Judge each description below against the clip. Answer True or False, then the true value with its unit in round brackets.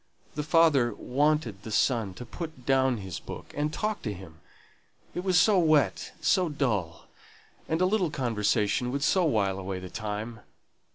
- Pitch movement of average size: False (7.0 semitones)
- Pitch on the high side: False (130 Hz)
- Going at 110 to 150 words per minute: False (165 wpm)